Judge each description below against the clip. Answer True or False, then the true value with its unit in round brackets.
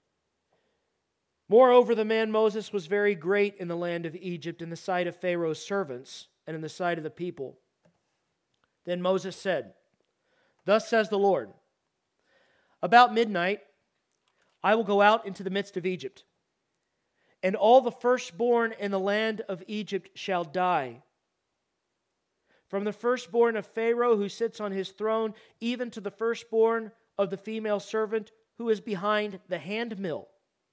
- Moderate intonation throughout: True (3.3 semitones)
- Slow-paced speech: False (150 wpm)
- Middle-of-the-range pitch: False (205 Hz)